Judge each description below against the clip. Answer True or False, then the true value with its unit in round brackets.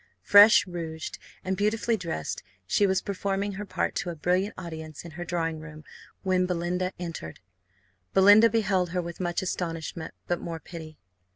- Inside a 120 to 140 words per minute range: False (160 wpm)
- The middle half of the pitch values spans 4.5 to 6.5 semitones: False (2.8 semitones)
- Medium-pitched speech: True (180 Hz)